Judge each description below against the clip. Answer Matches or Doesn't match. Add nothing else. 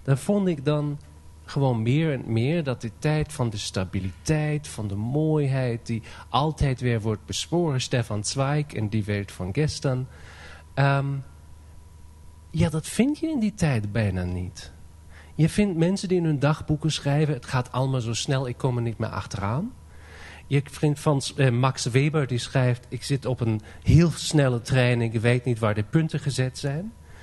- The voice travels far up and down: Matches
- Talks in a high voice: Doesn't match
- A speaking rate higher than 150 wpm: Matches